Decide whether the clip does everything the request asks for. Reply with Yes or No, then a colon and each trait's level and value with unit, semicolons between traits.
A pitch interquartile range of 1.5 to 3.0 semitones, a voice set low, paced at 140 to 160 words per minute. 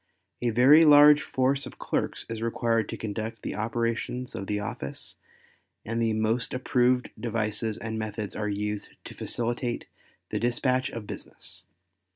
Yes: narrow, 2.5 semitones; low, 115 Hz; average, 150 wpm